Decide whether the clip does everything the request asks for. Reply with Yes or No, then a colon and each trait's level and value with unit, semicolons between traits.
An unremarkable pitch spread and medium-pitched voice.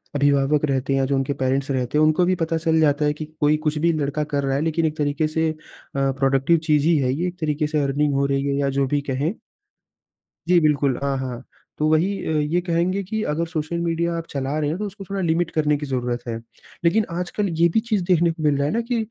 Yes: average, 3.3 semitones; medium, 150 Hz